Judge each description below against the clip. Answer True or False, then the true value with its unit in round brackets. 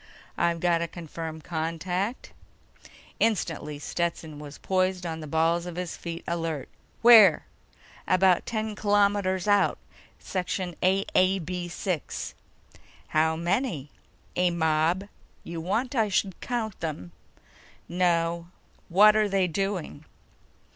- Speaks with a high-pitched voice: False (175 Hz)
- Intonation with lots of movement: False (3.0 semitones)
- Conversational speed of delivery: False (110 wpm)